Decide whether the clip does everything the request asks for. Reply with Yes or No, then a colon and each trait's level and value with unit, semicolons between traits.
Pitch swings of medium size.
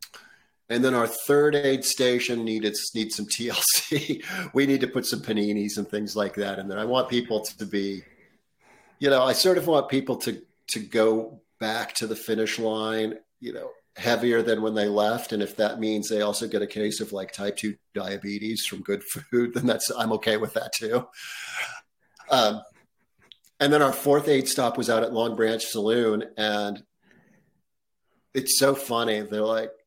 Yes: average, 3.1 semitones